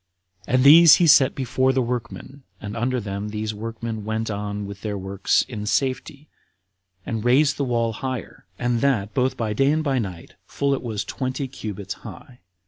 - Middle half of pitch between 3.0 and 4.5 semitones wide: Yes, average, 4.0 semitones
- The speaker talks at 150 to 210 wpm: Yes, average, 180 wpm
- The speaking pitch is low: Yes, low, 115 Hz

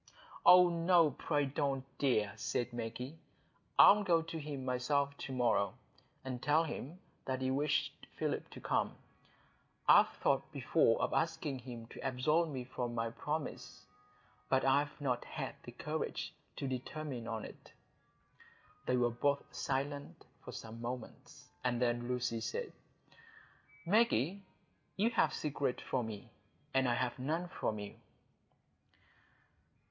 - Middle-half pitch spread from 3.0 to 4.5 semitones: Yes, average, 3.7 semitones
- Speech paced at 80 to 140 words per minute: Yes, slow, 135 wpm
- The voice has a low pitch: Yes, low, 130 Hz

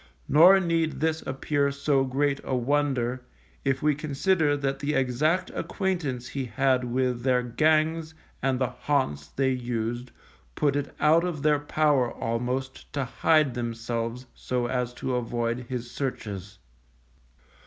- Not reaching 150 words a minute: Yes, average, 140 wpm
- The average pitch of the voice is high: No, low, 135 Hz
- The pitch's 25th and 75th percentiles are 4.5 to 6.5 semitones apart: No, average, 3.4 semitones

